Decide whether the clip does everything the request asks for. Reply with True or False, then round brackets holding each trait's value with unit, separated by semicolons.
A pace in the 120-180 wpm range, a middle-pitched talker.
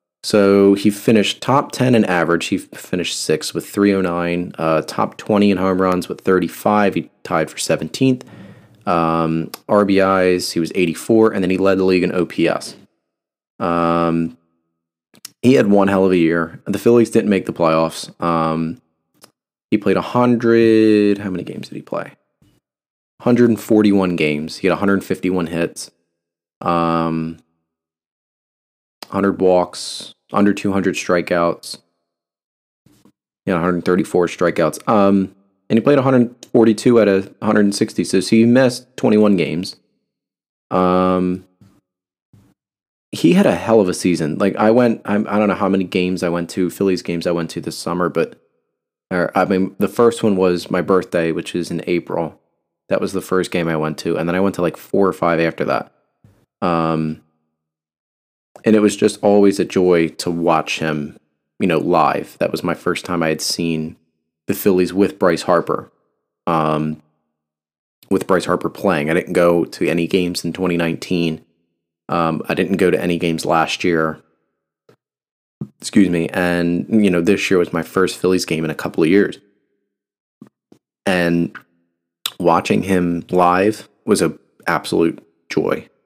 False (160 wpm; 90 Hz)